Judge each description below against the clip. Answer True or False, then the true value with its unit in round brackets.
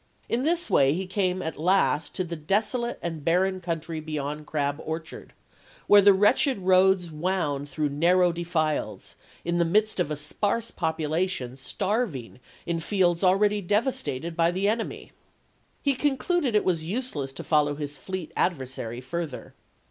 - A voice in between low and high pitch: True (175 Hz)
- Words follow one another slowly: False (160 wpm)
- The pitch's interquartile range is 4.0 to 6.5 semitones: True (4.6 semitones)